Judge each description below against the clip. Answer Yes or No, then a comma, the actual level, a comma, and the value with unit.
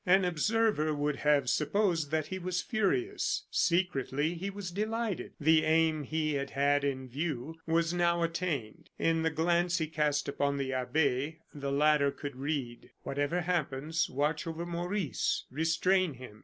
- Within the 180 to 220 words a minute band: No, average, 155 wpm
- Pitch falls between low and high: Yes, medium, 160 Hz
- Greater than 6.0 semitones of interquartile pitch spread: No, average, 3.6 semitones